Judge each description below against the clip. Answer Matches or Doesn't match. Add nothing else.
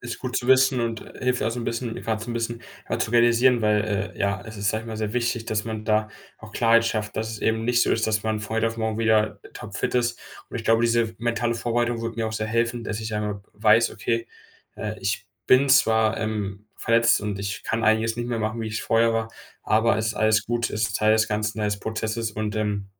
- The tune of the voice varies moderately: Doesn't match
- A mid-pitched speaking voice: Doesn't match